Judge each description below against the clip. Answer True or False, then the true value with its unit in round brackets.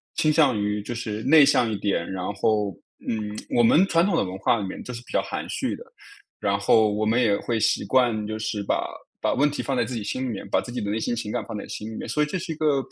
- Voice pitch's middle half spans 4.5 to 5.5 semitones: False (3.9 semitones)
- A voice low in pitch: True (110 Hz)